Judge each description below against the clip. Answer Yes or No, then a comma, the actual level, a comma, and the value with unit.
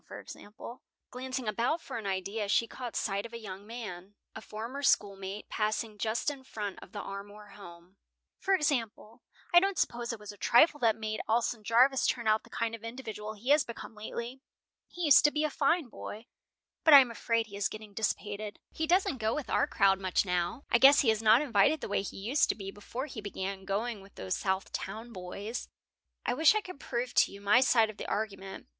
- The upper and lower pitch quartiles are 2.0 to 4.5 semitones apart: Yes, average, 3.8 semitones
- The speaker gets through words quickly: Yes, fast, 215 wpm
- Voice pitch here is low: No, high, 220 Hz